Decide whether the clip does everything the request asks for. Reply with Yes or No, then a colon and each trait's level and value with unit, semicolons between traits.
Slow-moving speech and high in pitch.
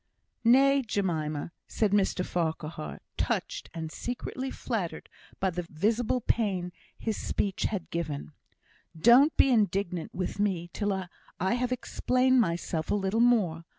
Yes: slow, 130 wpm; high, 195 Hz